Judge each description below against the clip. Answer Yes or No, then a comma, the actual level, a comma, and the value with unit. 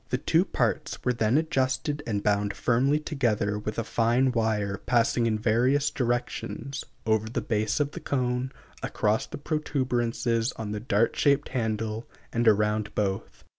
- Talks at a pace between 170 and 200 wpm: No, average, 155 wpm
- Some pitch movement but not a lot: Yes, average, 3.4 semitones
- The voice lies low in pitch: Yes, low, 115 Hz